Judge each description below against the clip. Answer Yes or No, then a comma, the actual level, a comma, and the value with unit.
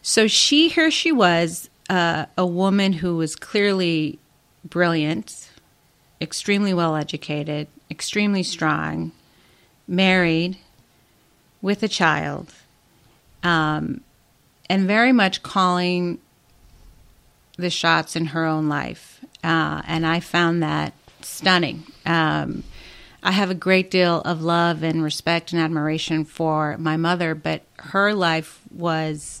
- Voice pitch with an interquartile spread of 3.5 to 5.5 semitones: No, average, 3.1 semitones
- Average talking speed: No, slow, 115 wpm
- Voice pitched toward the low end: No, medium, 170 Hz